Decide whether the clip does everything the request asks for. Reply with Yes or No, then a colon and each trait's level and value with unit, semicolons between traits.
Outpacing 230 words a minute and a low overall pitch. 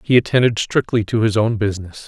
No: fast, 205 wpm; low, 110 Hz